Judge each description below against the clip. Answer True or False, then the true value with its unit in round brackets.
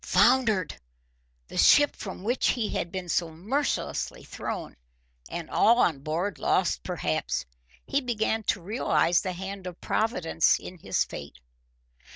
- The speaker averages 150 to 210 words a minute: False (140 wpm)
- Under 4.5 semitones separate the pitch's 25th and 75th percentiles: False (4.9 semitones)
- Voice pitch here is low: False (190 Hz)